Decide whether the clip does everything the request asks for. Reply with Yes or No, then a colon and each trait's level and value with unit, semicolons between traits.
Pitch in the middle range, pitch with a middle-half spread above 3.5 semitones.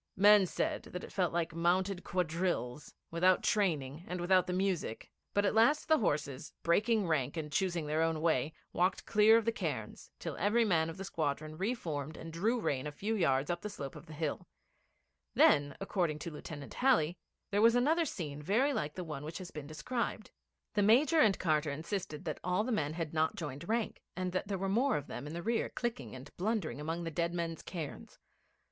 Yes: medium, 175 Hz; average, 5.0 semitones